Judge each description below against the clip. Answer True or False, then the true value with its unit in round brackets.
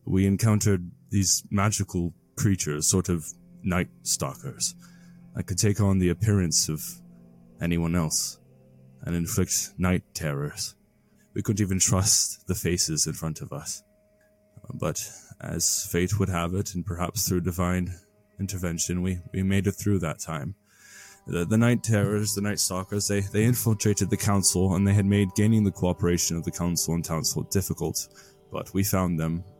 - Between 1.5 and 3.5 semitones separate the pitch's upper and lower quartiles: True (3.1 semitones)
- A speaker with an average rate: True (160 wpm)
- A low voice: True (95 Hz)